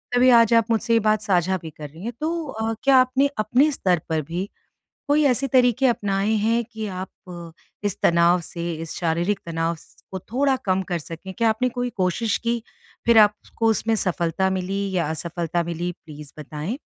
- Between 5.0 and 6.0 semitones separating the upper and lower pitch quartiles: Yes, wide, 5.5 semitones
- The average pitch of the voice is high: Yes, high, 195 Hz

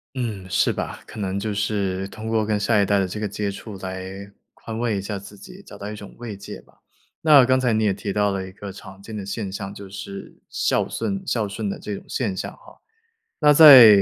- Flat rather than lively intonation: Yes, narrow, 2.3 semitones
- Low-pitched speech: Yes, low, 105 Hz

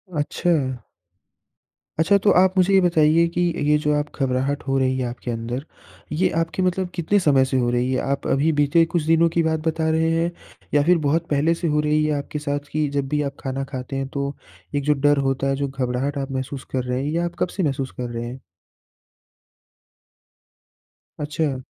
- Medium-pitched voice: Yes, medium, 145 Hz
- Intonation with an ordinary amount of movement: Yes, average, 3.4 semitones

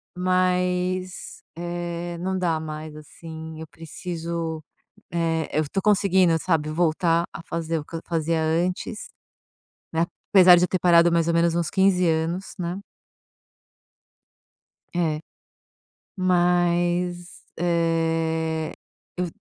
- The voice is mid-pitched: Yes, medium, 170 Hz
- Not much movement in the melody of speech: Yes, narrow, 1.8 semitones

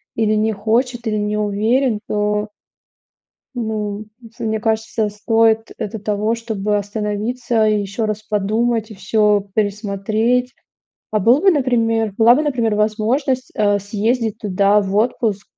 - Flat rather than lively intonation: Yes, narrow, 1.8 semitones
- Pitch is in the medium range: No, high, 215 Hz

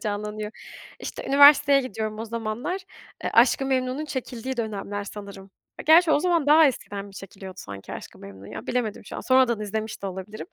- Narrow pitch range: No, average, 4.7 semitones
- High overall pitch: Yes, high, 220 Hz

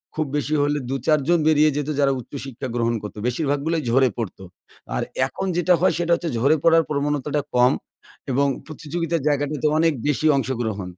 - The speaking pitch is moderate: Yes, medium, 145 Hz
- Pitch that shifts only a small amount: No, average, 3.1 semitones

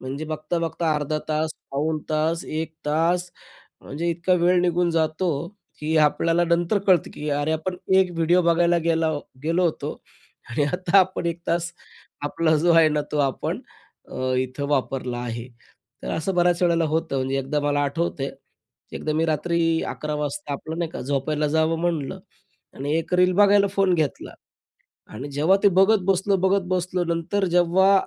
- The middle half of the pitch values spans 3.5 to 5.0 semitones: No, average, 2.8 semitones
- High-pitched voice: No, medium, 165 Hz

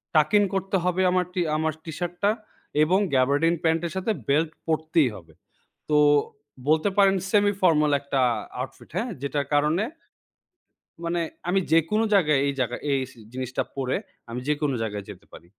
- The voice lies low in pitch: No, medium, 160 Hz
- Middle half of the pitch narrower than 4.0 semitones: No, average, 4.6 semitones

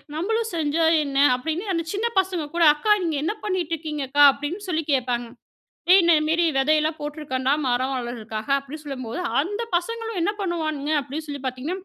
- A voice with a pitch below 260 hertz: No, very high, 310 Hz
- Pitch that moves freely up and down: No, average, 4.2 semitones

